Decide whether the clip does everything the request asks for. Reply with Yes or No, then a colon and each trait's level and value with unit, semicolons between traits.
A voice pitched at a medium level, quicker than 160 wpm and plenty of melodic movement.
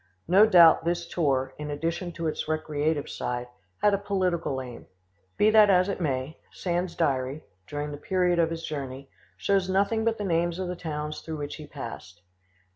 No: medium, 165 Hz; average, 185 wpm; average, 3.9 semitones